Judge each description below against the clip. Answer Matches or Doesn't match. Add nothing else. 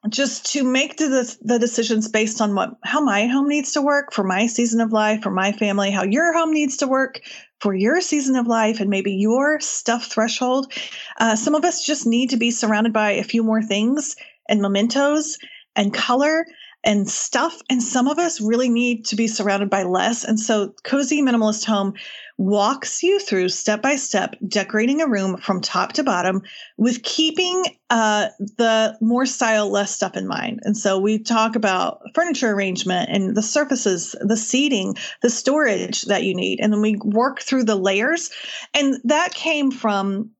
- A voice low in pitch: Doesn't match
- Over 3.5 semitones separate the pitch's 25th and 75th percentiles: Matches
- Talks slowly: Doesn't match